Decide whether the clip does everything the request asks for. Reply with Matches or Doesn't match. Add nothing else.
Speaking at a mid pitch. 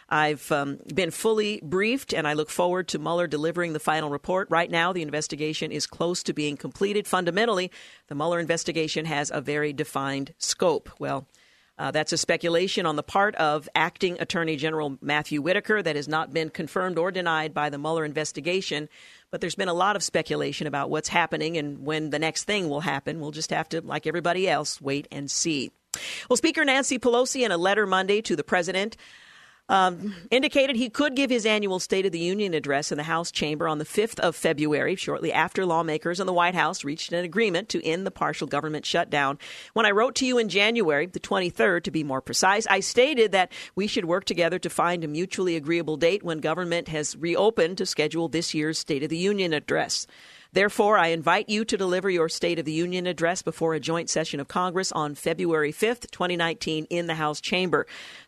Matches